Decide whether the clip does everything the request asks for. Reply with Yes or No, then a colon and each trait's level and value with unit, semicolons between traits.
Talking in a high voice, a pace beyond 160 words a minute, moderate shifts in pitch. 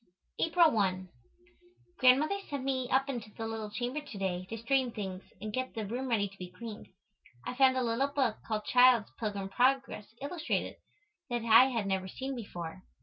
Yes: high, 235 Hz; average, 180 wpm; average, 4.2 semitones